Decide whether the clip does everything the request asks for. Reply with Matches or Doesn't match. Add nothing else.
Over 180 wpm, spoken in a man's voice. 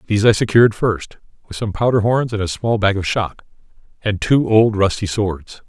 Matches